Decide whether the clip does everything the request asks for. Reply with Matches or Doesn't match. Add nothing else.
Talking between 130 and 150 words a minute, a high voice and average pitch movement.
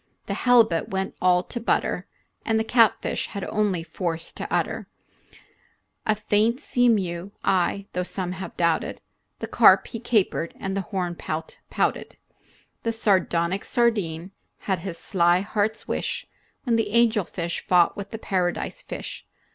Matches